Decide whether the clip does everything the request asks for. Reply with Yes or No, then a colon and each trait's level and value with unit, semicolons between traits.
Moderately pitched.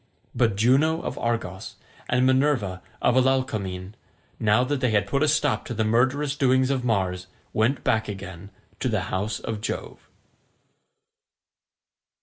No: low, 115 Hz